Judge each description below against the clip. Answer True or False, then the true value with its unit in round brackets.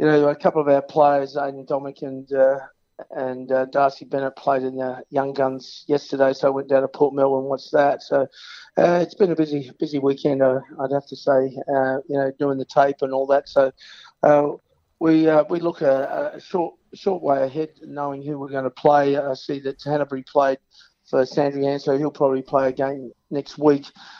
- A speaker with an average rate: False (210 wpm)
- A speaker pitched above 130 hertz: True (140 Hz)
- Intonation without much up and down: True (1.3 semitones)